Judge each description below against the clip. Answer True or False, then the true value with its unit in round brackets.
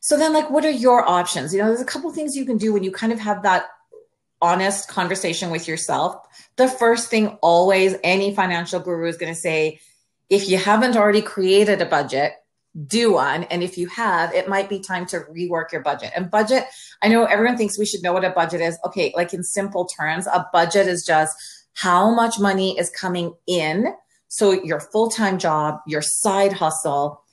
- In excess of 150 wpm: True (205 wpm)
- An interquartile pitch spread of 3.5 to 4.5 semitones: True (4.0 semitones)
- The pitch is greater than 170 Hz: True (190 Hz)